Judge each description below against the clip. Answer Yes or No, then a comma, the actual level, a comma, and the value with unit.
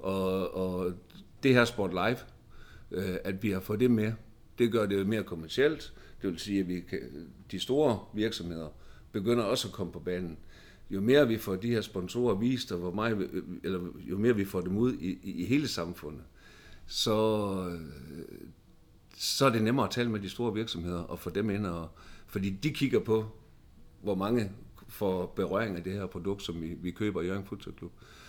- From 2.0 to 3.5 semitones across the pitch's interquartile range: No, average, 4.0 semitones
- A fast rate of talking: No, average, 195 wpm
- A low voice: Yes, low, 100 Hz